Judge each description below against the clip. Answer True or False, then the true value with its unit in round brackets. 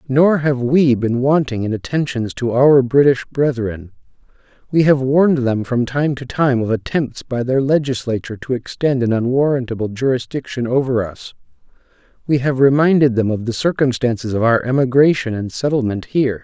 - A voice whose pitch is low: True (130 Hz)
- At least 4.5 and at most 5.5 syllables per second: True (5.2 syllables/s)